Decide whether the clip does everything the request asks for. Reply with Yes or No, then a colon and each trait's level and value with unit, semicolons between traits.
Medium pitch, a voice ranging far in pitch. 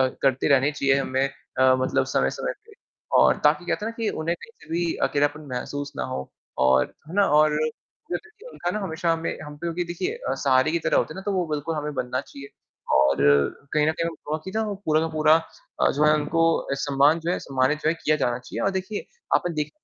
No: medium, 155 Hz; average, 3.7 semitones